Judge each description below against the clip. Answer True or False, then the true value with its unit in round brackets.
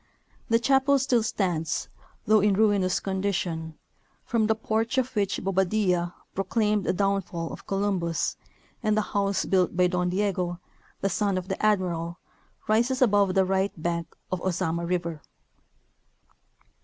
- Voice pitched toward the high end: True (195 Hz)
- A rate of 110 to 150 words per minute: True (145 wpm)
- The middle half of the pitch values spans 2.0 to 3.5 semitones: True (3.1 semitones)